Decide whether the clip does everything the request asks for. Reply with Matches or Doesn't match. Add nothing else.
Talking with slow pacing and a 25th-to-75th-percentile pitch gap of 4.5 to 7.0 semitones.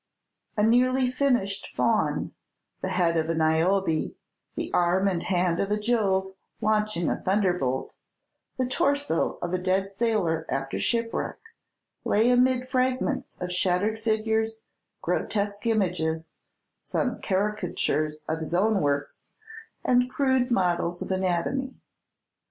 Matches